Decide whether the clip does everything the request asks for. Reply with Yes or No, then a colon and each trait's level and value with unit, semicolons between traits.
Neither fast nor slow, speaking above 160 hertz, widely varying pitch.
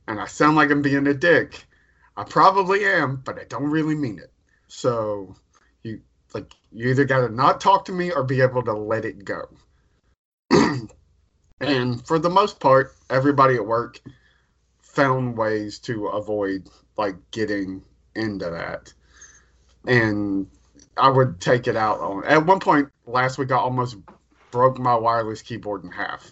No: average, 160 wpm; low, 125 Hz; wide, 5.7 semitones